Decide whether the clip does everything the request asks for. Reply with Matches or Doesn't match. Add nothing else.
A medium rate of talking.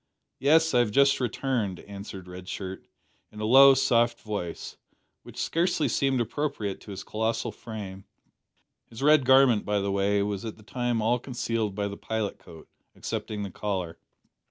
Matches